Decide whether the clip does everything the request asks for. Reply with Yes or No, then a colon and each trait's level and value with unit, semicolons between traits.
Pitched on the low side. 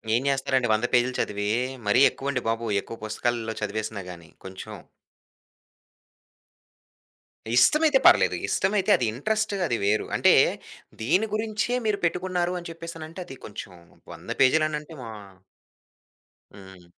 Yes: low, 130 Hz